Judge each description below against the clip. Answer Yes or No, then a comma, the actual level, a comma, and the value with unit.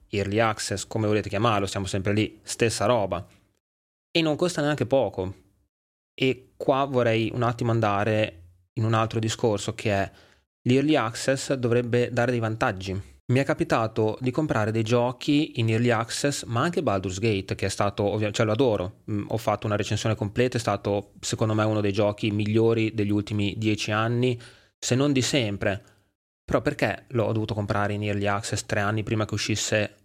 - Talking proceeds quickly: Yes, fast, 180 wpm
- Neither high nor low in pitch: No, low, 110 Hz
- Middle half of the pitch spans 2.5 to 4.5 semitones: Yes, average, 3.0 semitones